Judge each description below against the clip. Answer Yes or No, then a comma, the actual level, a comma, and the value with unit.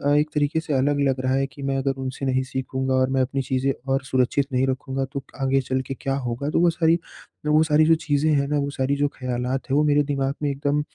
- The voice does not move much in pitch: Yes, narrow, 1.8 semitones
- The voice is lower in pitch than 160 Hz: Yes, low, 135 Hz